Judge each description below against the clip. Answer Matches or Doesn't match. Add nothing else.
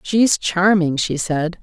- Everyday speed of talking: Matches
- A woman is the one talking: Matches